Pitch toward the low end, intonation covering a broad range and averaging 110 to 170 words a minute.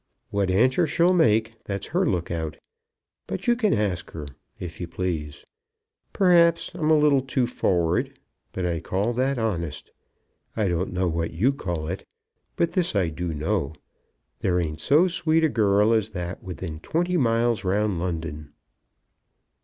Yes: low, 100 Hz; wide, 7.9 semitones; average, 160 wpm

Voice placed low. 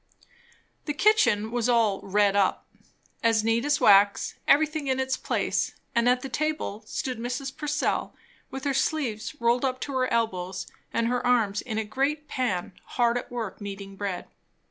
No: high, 240 Hz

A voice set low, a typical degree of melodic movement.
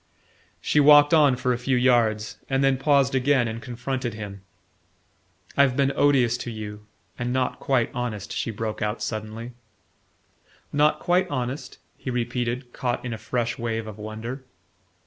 Yes: low, 125 Hz; average, 3.0 semitones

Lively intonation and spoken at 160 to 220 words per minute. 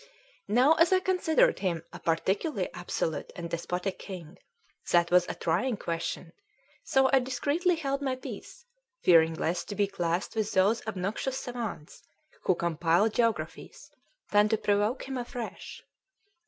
No: wide, 7.1 semitones; average, 140 wpm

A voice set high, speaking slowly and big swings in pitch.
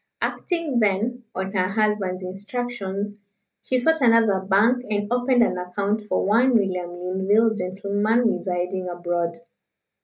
No: high, 205 Hz; slow, 125 wpm; average, 3.8 semitones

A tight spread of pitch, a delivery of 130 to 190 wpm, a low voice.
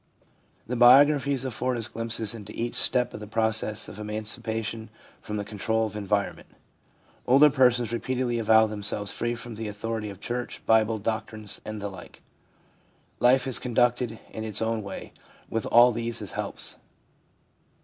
Yes: narrow, 2.2 semitones; average, 160 wpm; low, 115 Hz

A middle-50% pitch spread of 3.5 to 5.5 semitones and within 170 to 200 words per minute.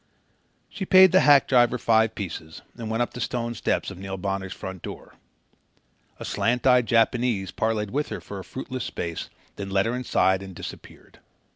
Yes: average, 4.4 semitones; average, 180 wpm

